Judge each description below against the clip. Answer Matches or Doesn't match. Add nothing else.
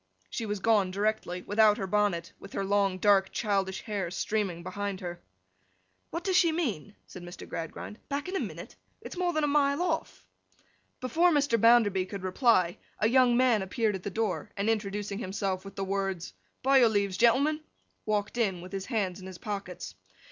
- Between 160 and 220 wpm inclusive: Matches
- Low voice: Doesn't match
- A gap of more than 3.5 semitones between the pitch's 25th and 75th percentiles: Matches